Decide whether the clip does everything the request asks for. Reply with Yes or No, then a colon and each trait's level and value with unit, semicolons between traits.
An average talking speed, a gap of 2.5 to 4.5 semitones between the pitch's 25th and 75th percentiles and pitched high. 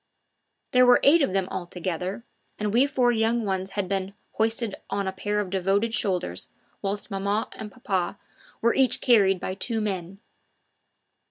Yes: average, 165 wpm; average, 3.1 semitones; high, 200 Hz